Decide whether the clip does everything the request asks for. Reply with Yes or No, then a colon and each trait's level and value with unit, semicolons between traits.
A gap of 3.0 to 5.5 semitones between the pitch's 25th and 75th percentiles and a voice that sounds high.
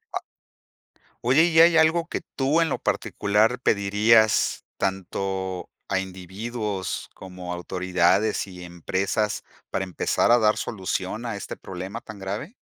No: average, 3.9 semitones; low, 100 Hz